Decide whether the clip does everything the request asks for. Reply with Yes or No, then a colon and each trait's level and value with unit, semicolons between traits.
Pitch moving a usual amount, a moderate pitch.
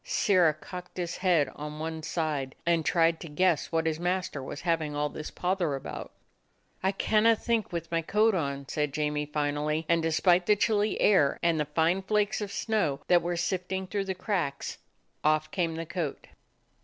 Yes: average, 3.6 semitones; medium, 170 Hz